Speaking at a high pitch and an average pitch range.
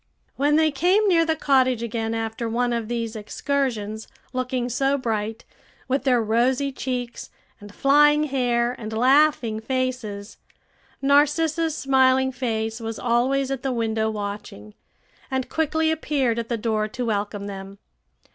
Yes: high, 245 Hz; average, 3.7 semitones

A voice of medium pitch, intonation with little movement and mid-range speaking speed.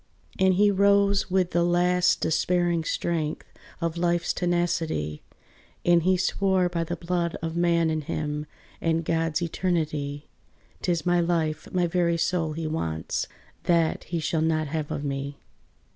Yes: medium, 170 Hz; narrow, 2.0 semitones; average, 145 wpm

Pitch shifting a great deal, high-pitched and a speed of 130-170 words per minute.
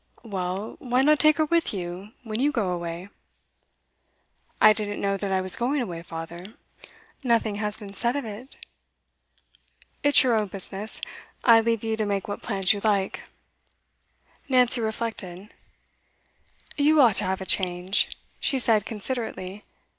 No: average, 3.9 semitones; high, 210 Hz; average, 150 wpm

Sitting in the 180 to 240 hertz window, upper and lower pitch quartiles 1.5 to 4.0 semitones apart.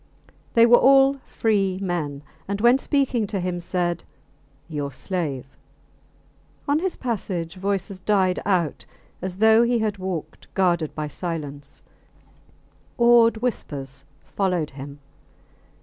No: medium, 185 Hz; wide, 5.6 semitones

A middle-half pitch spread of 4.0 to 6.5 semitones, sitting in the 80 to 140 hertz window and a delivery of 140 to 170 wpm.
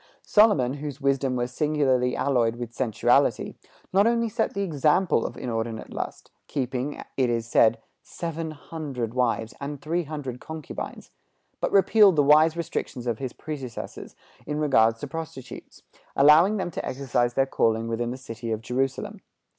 Yes: average, 4.3 semitones; low, 135 Hz; average, 155 wpm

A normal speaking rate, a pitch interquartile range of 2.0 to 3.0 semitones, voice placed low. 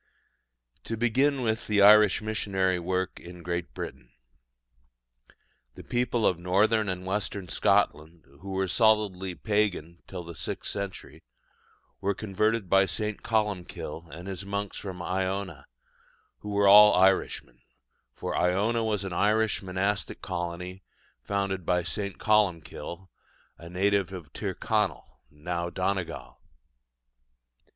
No: slow, 120 wpm; average, 2.7 semitones; very low, 95 Hz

